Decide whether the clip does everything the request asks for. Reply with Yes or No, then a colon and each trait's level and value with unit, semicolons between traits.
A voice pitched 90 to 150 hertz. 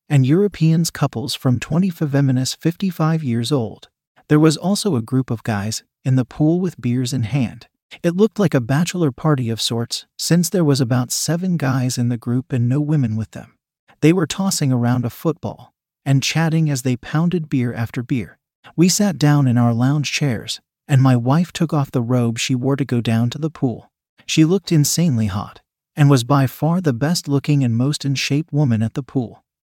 Yes: medium, 140 Hz